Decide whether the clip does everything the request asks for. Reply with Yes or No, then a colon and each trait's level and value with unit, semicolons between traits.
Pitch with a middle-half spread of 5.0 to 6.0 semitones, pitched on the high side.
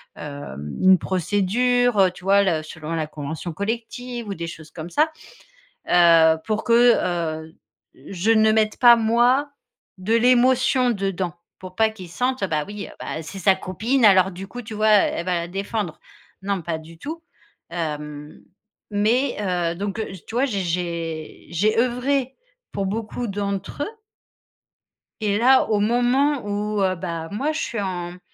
Yes: wide, 5.5 semitones; high, 200 Hz